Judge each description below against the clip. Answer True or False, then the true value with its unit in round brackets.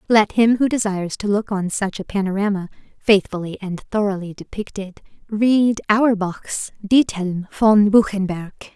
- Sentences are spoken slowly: True (130 wpm)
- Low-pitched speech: False (205 Hz)